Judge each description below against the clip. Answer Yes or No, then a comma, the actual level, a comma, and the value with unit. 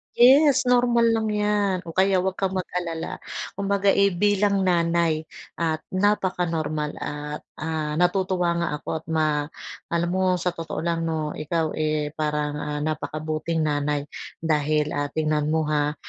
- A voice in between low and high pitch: Yes, medium, 165 Hz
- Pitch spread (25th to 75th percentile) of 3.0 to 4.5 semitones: Yes, average, 3.6 semitones